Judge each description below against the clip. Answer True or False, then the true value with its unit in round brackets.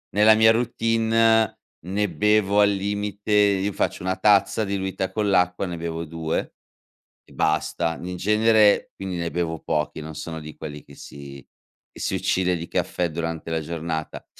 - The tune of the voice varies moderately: True (4.0 semitones)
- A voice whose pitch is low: True (95 Hz)